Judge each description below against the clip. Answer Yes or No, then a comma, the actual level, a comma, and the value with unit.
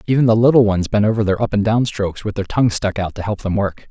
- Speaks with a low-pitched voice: Yes, low, 105 Hz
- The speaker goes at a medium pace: No, fast, 310 wpm